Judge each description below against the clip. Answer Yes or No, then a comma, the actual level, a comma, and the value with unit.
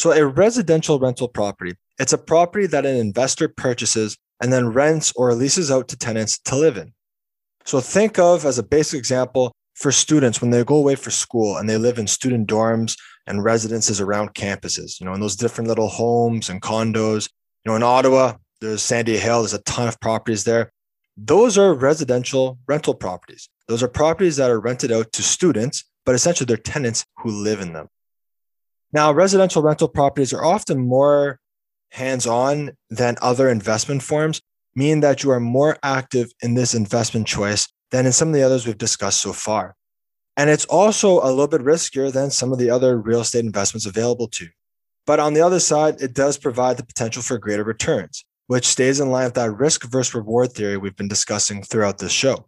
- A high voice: No, low, 125 Hz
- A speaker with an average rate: Yes, average, 195 wpm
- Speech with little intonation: No, average, 4.0 semitones